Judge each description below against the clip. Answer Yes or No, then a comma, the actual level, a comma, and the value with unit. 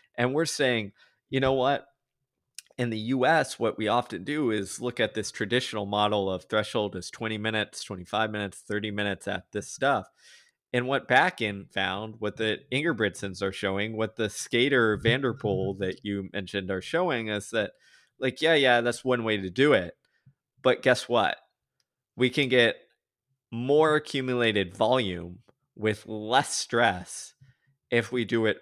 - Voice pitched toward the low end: Yes, low, 110 Hz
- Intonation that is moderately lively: Yes, average, 3.7 semitones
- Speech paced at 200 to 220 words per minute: No, average, 165 wpm